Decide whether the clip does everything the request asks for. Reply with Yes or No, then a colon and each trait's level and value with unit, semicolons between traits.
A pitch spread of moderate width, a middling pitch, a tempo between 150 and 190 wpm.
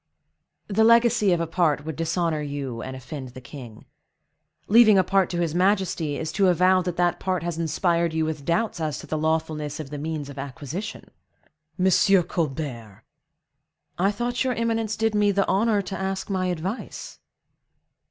Yes: average, 4.4 semitones; medium, 170 Hz; average, 170 wpm